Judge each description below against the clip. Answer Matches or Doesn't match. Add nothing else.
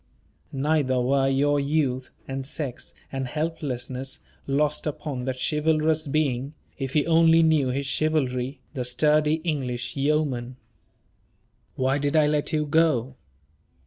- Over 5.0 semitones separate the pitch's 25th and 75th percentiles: Doesn't match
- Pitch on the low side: Doesn't match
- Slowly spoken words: Matches